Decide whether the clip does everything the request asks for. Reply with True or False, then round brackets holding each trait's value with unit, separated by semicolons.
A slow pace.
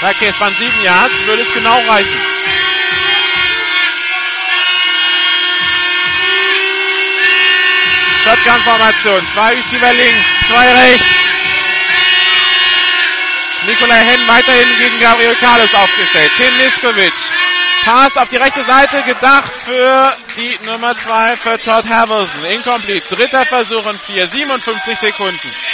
True (105 wpm)